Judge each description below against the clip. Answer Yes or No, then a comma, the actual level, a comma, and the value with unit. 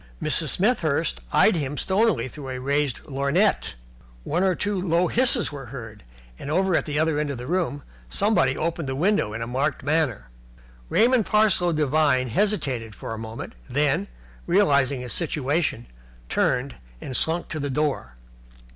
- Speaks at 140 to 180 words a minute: Yes, average, 160 wpm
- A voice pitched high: No, medium, 145 Hz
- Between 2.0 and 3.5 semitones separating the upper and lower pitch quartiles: No, average, 5.3 semitones